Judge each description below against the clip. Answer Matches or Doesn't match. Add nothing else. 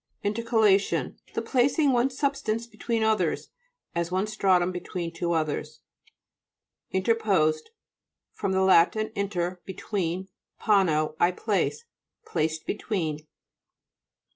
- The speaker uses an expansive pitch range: Doesn't match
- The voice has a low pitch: Doesn't match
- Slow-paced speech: Matches